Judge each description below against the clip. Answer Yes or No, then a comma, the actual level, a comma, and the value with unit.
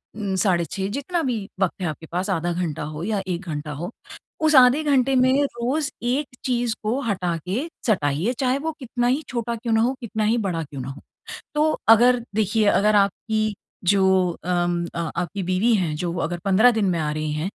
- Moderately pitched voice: No, high, 205 Hz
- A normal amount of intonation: No, wide, 5.8 semitones